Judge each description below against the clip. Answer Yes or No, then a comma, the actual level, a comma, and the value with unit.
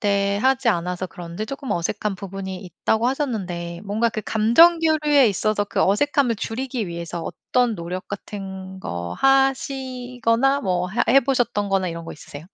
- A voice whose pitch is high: Yes, high, 210 Hz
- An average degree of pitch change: No, wide, 5.7 semitones